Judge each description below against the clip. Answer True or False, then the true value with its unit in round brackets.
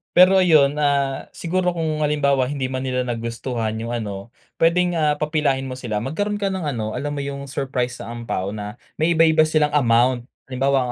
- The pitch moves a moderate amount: True (4.2 semitones)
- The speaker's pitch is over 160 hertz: False (140 Hz)